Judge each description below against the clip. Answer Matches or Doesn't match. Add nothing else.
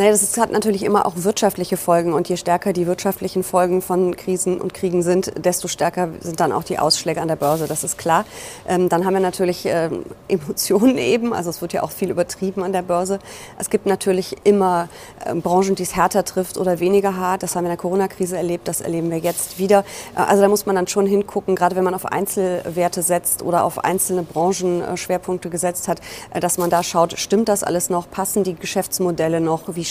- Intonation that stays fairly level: Matches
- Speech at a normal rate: Doesn't match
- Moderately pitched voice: Matches